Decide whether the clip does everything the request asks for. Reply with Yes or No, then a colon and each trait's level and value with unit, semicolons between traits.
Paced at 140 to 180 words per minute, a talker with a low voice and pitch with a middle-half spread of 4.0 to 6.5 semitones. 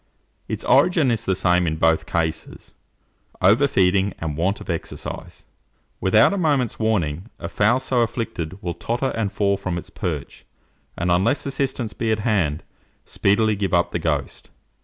Yes: average, 160 wpm; low, 100 Hz; average, 4.9 semitones